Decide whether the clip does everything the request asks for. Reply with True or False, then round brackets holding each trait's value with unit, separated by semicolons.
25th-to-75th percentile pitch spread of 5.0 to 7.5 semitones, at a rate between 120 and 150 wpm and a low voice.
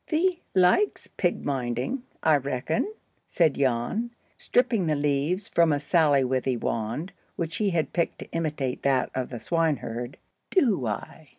False (5.5 semitones; 140 wpm; 150 Hz)